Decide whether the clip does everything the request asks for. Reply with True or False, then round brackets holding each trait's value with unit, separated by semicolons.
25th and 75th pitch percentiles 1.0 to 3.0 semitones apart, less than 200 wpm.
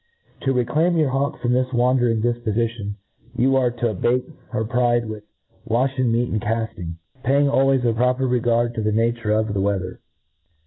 True (2.5 semitones; 165 wpm)